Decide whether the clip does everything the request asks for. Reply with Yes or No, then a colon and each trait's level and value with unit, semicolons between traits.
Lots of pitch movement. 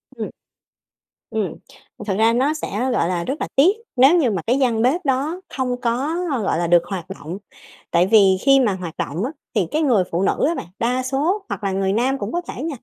Yes: wide, 6.0 semitones